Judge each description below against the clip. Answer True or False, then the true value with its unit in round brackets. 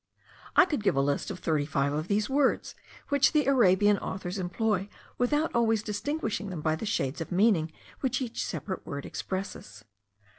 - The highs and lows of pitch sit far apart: True (6.8 semitones)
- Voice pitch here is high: True (200 Hz)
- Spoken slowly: False (175 wpm)